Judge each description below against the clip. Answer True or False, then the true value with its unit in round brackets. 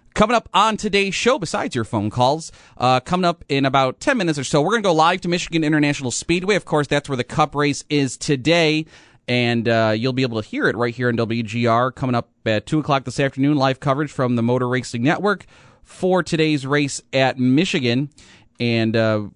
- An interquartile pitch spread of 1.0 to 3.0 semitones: False (4.3 semitones)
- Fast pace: True (215 wpm)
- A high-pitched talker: False (135 Hz)